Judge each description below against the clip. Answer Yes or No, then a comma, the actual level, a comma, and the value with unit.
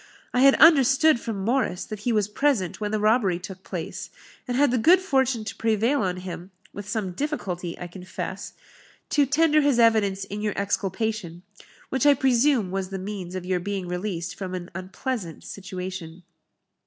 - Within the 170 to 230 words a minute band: Yes, average, 175 wpm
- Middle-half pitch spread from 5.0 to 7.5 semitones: Yes, wide, 5.4 semitones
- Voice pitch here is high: Yes, high, 205 Hz